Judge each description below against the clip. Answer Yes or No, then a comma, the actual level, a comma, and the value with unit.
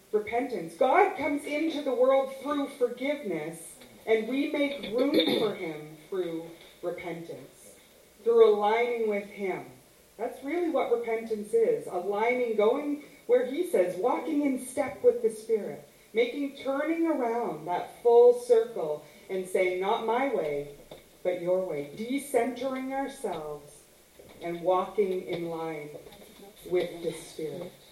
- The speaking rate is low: Yes, slow, 125 wpm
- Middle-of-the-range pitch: No, high, 235 Hz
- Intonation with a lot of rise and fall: Yes, wide, 7.7 semitones